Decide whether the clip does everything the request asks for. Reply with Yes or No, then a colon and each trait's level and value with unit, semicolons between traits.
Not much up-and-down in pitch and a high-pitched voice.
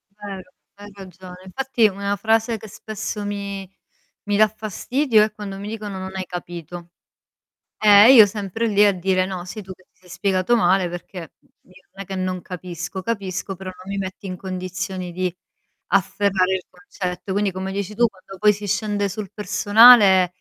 Yes: narrow, 2.0 semitones; high, 195 Hz